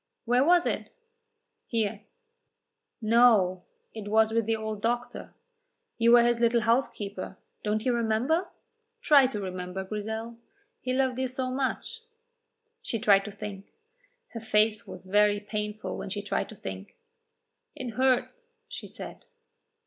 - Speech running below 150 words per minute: Yes, average, 140 wpm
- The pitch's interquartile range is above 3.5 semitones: No, average, 2.9 semitones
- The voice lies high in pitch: Yes, high, 220 Hz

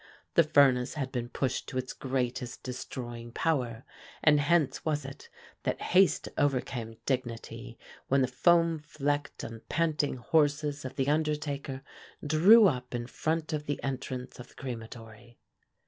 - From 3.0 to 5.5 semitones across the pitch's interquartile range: Yes, average, 3.3 semitones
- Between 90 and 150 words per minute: Yes, average, 145 wpm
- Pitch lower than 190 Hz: Yes, low, 135 Hz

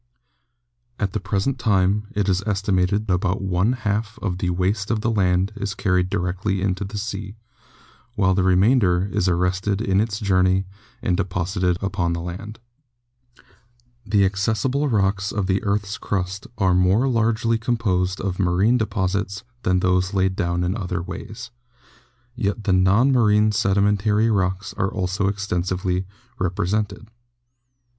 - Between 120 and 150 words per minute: Yes, average, 145 wpm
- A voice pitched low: Yes, low, 100 Hz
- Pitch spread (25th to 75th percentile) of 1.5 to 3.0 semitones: Yes, narrow, 2.4 semitones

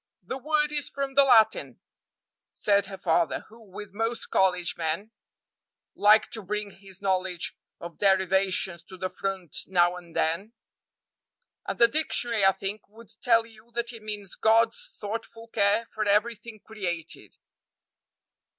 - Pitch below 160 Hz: No, high, 205 Hz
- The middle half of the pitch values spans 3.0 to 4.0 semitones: Yes, average, 3.3 semitones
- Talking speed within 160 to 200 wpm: No, average, 140 wpm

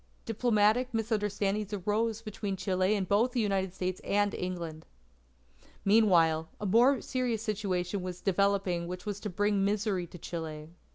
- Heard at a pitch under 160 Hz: No, high, 200 Hz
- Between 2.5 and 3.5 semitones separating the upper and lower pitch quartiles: Yes, average, 2.8 semitones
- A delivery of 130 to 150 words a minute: Yes, average, 145 wpm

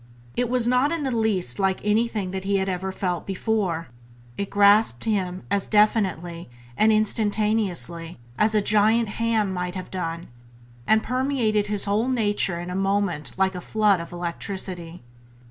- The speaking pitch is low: No, high, 200 Hz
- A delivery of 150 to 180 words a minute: Yes, average, 160 wpm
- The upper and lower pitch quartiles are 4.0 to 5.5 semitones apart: No, average, 3.3 semitones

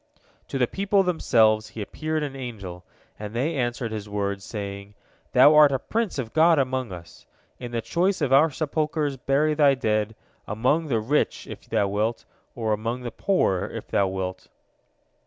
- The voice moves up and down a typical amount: No, wide, 6.0 semitones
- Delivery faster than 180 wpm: No, average, 175 wpm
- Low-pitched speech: Yes, low, 125 Hz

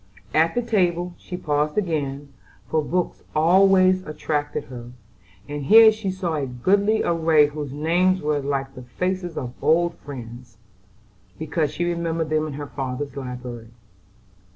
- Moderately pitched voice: Yes, medium, 155 Hz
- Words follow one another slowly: No, average, 145 wpm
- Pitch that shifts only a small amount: No, average, 4.3 semitones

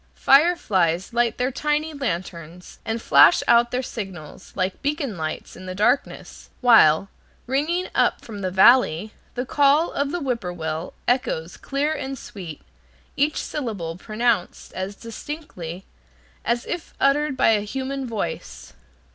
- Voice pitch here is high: Yes, high, 235 Hz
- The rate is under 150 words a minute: Yes, average, 140 wpm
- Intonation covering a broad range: Yes, wide, 7.0 semitones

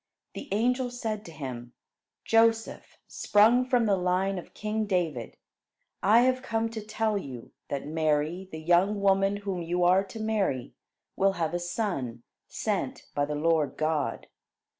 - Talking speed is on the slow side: No, average, 155 wpm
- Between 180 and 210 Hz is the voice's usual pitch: Yes, high, 190 Hz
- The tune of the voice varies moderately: No, wide, 5.7 semitones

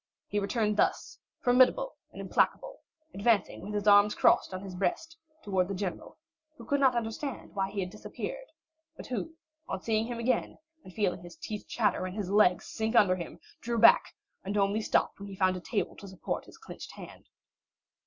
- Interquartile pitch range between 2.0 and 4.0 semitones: Yes, average, 3.6 semitones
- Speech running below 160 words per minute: No, average, 190 wpm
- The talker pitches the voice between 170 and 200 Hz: No, high, 210 Hz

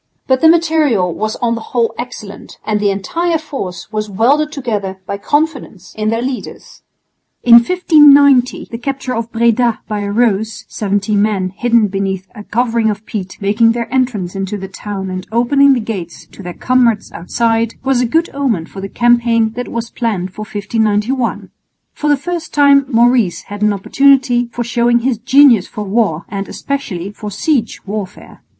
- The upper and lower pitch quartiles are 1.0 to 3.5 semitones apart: No, average, 3.9 semitones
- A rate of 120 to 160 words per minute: No, average, 170 wpm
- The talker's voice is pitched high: Yes, high, 230 Hz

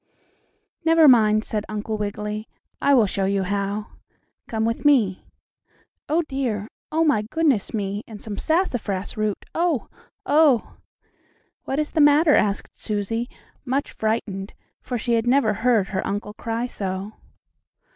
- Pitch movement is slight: No, average, 4.9 semitones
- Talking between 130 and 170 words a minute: Yes, average, 140 wpm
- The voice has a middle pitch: No, high, 220 Hz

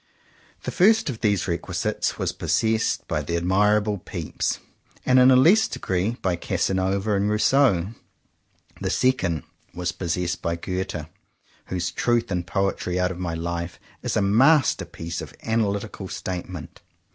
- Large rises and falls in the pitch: No, average, 4.1 semitones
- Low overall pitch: Yes, very low, 95 Hz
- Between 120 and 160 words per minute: Yes, average, 140 wpm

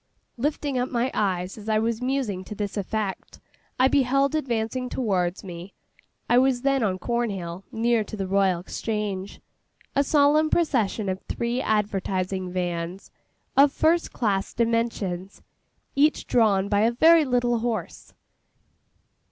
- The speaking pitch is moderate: No, high, 220 Hz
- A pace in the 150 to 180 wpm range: No, slow, 135 wpm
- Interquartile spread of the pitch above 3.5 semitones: Yes, average, 4.8 semitones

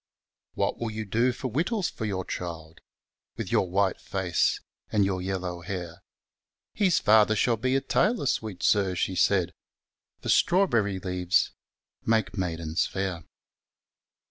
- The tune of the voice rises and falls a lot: No, average, 4.1 semitones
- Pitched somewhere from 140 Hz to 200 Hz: No, low, 100 Hz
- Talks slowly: Yes, slow, 125 wpm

